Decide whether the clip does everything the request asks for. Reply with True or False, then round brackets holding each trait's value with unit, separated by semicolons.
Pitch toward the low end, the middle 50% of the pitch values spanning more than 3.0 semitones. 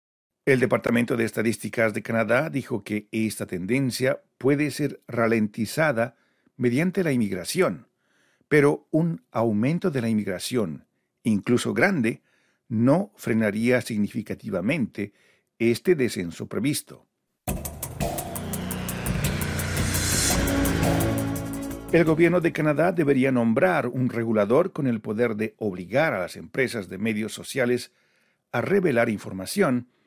True (115 Hz; 3.8 semitones)